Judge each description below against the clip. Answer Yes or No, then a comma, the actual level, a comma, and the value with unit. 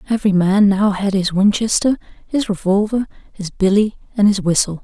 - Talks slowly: No, average, 160 wpm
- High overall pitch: Yes, high, 200 Hz